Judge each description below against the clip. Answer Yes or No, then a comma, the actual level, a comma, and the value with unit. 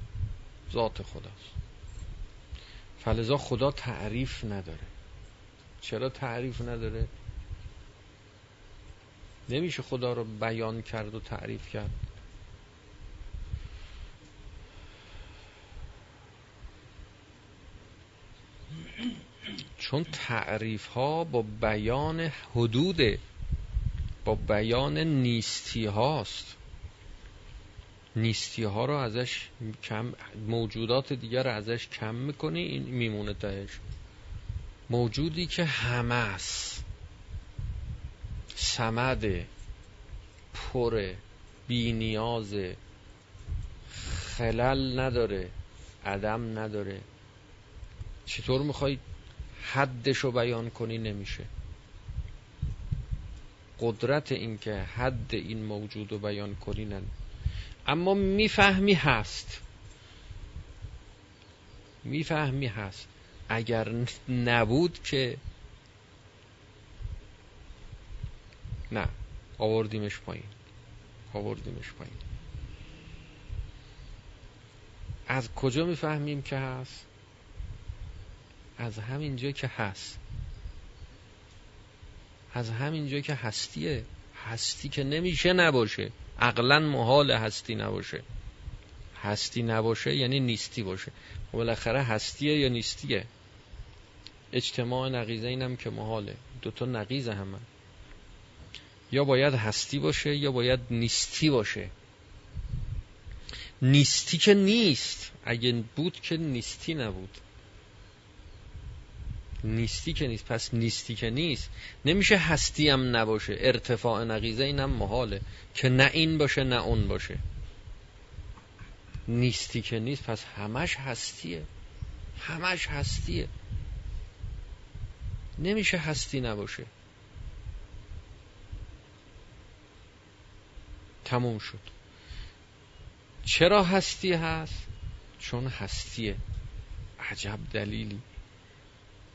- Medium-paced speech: No, slow, 80 wpm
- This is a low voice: Yes, low, 110 Hz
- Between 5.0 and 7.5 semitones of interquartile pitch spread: No, average, 3.7 semitones